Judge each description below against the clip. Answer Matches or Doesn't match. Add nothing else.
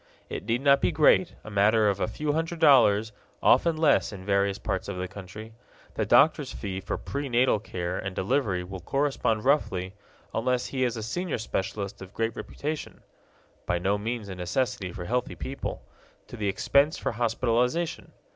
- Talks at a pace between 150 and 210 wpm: Matches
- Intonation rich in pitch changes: Matches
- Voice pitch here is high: Doesn't match